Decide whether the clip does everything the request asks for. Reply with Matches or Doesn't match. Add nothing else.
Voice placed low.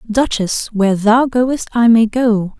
Doesn't match